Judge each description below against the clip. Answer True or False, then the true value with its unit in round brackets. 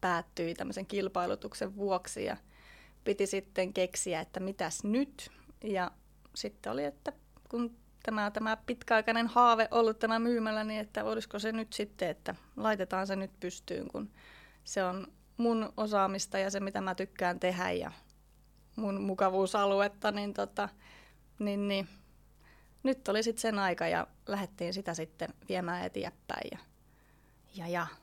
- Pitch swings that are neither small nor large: True (3.1 semitones)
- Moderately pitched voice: False (195 Hz)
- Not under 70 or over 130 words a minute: False (140 wpm)